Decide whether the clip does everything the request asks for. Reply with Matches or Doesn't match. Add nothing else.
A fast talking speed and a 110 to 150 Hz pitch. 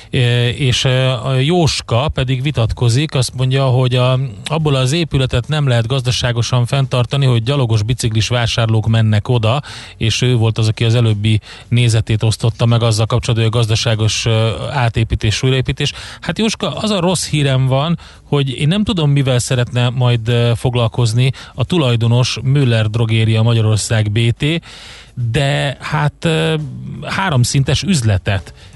Doesn't match